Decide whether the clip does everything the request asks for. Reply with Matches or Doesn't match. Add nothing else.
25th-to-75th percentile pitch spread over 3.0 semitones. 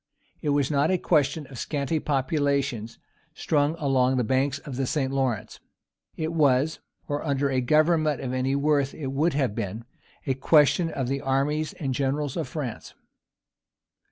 Doesn't match